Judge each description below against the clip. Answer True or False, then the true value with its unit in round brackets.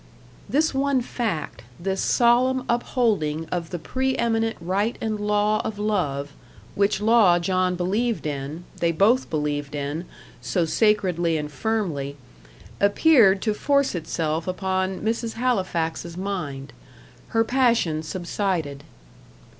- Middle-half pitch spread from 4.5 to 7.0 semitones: True (5.6 semitones)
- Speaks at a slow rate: True (120 wpm)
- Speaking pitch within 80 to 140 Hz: False (190 Hz)